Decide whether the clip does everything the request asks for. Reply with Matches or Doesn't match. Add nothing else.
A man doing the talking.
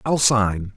Matches